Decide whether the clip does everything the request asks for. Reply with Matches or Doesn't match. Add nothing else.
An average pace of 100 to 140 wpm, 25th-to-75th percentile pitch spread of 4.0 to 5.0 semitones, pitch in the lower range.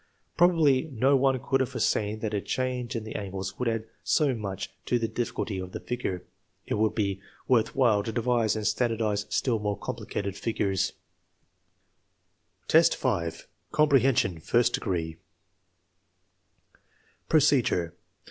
Matches